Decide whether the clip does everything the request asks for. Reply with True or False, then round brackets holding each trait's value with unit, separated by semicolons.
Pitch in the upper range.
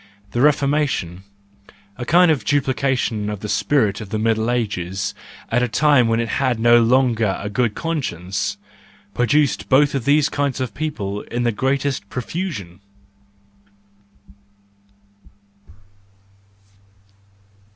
False (120 Hz)